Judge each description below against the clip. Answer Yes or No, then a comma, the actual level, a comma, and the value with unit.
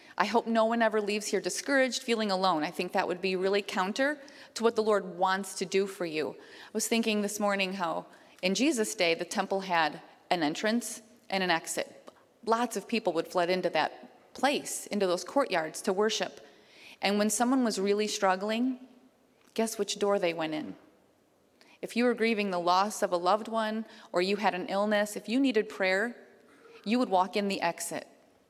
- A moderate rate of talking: Yes, average, 195 wpm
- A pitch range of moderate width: Yes, average, 3.4 semitones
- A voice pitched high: Yes, high, 205 Hz